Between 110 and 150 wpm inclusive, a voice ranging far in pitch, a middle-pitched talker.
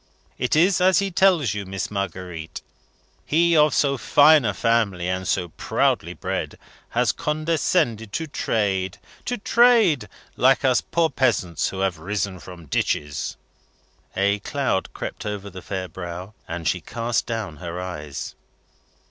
No: average, 145 wpm; wide, 8.3 semitones; low, 105 Hz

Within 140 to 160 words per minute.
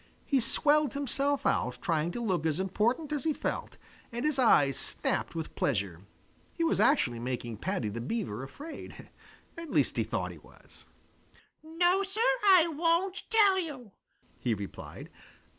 Yes: average, 155 wpm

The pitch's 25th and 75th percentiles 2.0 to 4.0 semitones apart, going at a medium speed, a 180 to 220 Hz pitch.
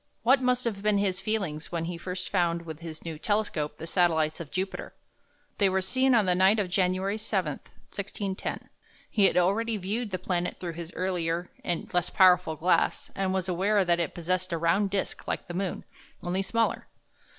Yes: average, 2.8 semitones; average, 190 wpm; medium, 185 Hz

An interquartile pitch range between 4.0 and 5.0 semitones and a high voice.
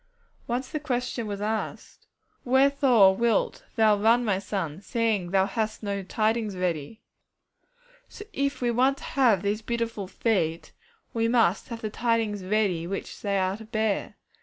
No: average, 3.1 semitones; high, 220 Hz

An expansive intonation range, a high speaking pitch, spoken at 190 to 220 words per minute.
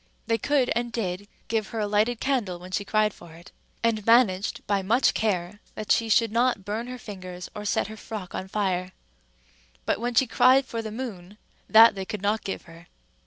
No: average, 3.4 semitones; high, 215 Hz; fast, 205 wpm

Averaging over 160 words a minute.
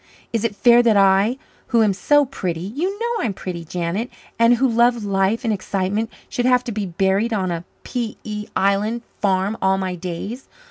Yes: average, 190 wpm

